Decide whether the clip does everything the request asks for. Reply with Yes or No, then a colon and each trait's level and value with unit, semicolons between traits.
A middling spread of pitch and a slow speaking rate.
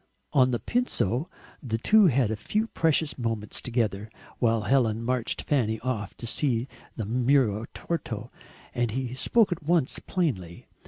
No: average, 4.6 semitones; average, 150 wpm